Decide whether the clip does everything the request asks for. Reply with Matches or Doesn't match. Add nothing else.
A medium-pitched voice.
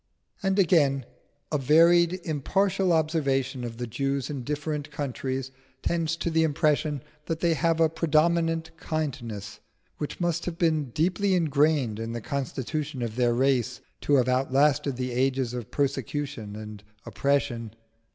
Matches